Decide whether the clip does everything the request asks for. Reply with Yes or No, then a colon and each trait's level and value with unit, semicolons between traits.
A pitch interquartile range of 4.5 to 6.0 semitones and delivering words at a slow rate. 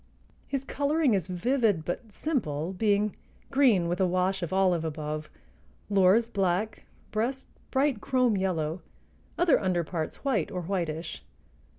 Yes: wide, 5.5 semitones; slow, 130 wpm